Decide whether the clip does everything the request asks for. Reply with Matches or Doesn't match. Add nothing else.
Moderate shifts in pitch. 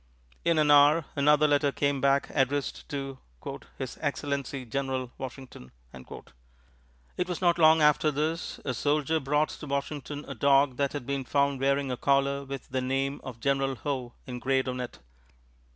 Doesn't match